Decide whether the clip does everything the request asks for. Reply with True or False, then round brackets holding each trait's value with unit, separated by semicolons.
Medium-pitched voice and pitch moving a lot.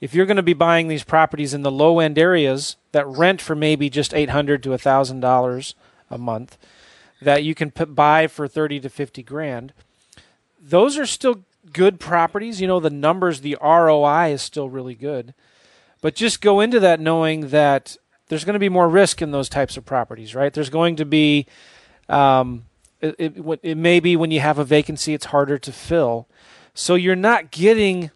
False (155 Hz; 3.3 semitones)